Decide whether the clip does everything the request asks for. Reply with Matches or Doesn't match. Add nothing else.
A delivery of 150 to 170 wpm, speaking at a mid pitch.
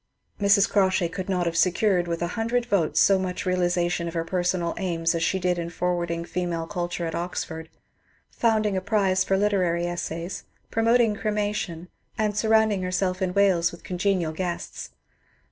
Matches